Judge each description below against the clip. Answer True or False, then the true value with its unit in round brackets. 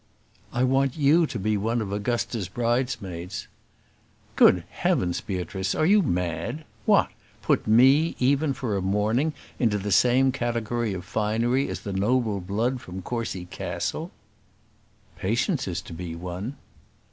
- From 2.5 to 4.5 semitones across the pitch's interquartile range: False (5.1 semitones)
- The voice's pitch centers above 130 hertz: False (115 Hz)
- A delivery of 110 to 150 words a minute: True (140 wpm)